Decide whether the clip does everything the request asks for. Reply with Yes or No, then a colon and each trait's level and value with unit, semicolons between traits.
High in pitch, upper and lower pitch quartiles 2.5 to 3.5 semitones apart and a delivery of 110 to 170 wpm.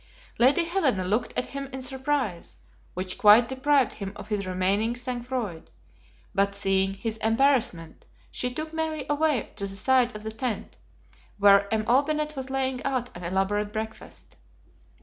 No: high, 235 Hz; average, 5.1 semitones; average, 155 wpm